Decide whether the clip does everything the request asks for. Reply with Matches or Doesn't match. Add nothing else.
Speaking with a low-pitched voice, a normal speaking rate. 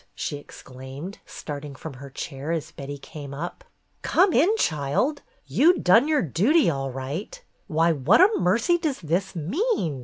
Doesn't match